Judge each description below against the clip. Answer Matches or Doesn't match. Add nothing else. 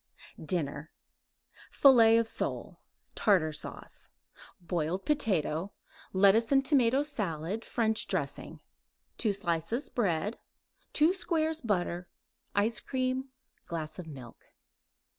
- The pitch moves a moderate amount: Doesn't match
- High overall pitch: Matches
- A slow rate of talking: Matches